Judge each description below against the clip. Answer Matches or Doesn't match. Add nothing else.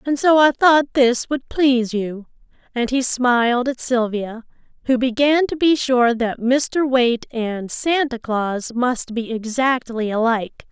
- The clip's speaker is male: Doesn't match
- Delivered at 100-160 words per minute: Matches